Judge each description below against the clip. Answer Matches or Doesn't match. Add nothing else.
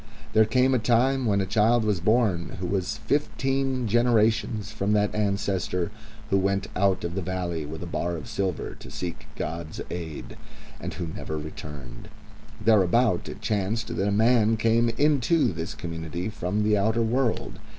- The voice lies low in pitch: Matches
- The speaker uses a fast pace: Doesn't match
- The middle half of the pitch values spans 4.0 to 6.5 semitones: Matches